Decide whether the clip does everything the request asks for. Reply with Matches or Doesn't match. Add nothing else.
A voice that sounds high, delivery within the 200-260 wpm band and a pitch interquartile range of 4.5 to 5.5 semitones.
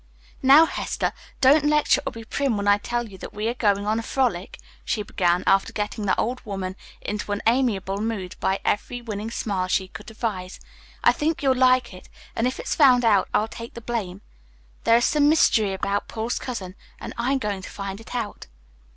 Doesn't match